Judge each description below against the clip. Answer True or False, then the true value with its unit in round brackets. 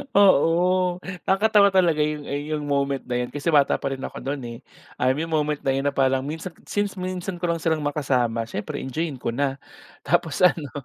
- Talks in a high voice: False (150 Hz)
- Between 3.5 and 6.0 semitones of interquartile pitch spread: True (4.3 semitones)